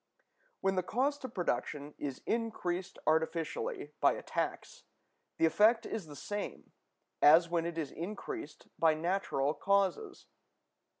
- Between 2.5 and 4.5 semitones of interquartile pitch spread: No, average, 4.9 semitones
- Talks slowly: Yes, slow, 130 wpm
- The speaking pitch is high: No, medium, 175 Hz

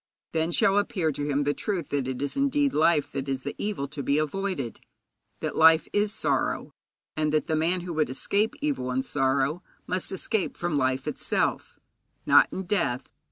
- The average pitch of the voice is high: No, medium, 155 Hz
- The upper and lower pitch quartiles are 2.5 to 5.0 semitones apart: No, wide, 5.4 semitones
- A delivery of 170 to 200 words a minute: Yes, average, 185 wpm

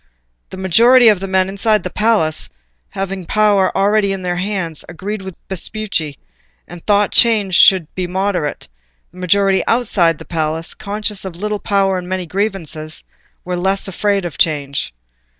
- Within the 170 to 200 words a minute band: No, average, 155 wpm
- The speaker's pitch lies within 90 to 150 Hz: No, high, 190 Hz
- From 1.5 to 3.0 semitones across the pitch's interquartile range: Yes, average, 2.7 semitones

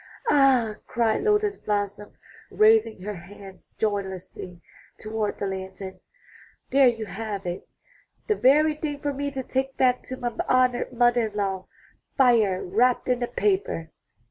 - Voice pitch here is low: No, high, 230 Hz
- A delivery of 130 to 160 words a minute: Yes, average, 145 wpm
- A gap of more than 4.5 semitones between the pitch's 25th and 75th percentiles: Yes, average, 5.1 semitones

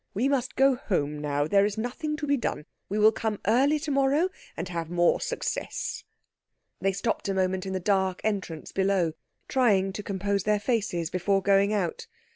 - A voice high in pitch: Yes, high, 200 Hz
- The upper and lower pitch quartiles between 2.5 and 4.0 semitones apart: No, average, 4.5 semitones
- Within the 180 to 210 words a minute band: Yes, average, 185 wpm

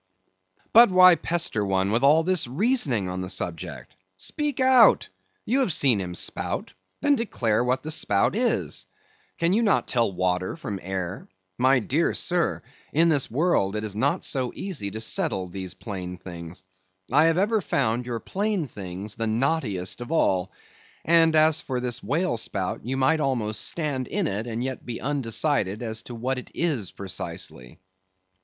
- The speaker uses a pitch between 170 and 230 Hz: No, low, 125 Hz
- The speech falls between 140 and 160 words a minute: No, average, 170 wpm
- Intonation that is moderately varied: No, wide, 8.4 semitones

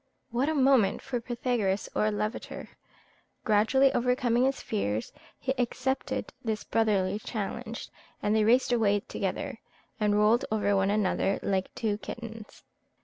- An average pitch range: Yes, average, 3.1 semitones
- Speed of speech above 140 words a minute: No, slow, 135 wpm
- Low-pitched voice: No, high, 220 Hz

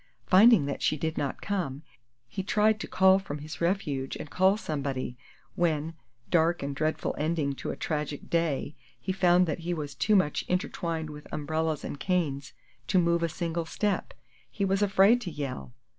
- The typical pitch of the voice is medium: Yes, medium, 165 Hz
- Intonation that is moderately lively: Yes, average, 4.2 semitones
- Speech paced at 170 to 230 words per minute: Yes, average, 175 wpm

